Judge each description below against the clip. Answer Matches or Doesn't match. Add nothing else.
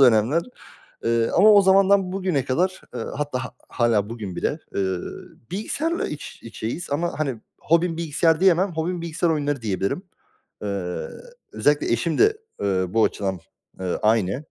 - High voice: Doesn't match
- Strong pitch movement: Matches